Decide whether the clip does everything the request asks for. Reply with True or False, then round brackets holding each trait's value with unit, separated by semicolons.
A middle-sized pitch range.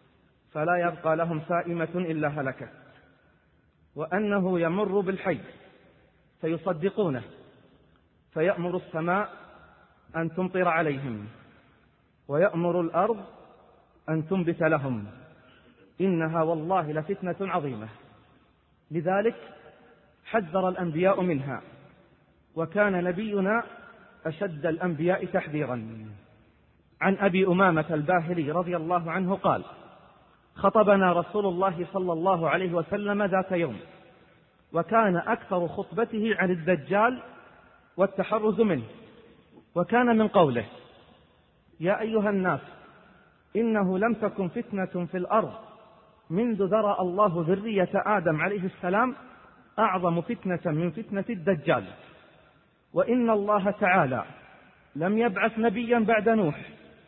True (3.8 semitones)